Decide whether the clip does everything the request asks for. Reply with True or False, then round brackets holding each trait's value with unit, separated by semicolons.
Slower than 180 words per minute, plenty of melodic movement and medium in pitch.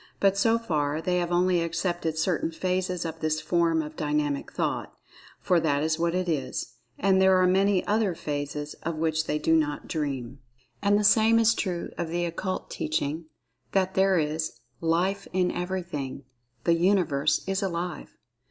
False (160 wpm; 3.4 semitones; 170 Hz)